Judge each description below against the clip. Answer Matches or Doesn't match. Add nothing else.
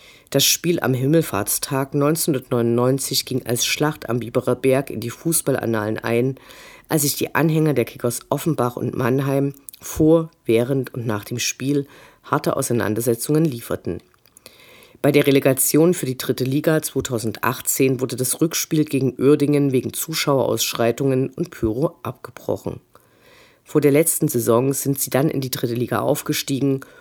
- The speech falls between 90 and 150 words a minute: Matches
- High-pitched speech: Doesn't match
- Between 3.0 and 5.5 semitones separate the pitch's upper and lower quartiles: Matches